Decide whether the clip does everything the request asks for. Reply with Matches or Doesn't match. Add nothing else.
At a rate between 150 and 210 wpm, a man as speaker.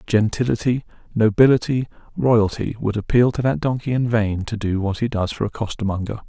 Matches